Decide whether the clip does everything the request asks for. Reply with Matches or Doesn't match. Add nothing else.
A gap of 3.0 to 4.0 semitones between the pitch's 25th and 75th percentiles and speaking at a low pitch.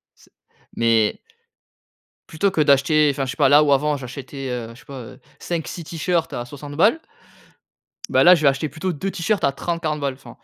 Doesn't match